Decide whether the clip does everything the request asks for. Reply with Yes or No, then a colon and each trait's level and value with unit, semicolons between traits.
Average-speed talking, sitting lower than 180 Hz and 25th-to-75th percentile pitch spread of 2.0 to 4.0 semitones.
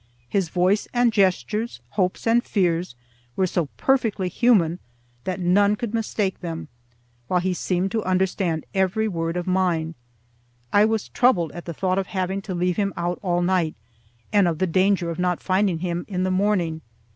No: average, 175 wpm; medium, 185 Hz; narrow, 2.6 semitones